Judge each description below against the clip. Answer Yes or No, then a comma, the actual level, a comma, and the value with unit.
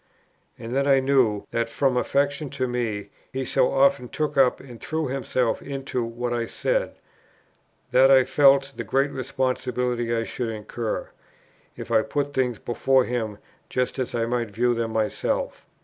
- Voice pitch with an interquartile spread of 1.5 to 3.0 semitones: Yes, narrow, 2.6 semitones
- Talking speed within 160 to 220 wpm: Yes, average, 165 wpm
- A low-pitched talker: Yes, low, 125 Hz